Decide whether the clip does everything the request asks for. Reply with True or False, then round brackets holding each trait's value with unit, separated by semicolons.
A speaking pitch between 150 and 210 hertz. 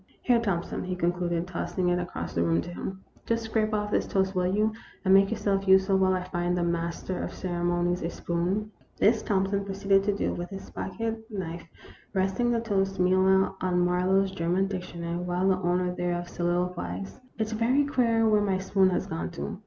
True (190 Hz)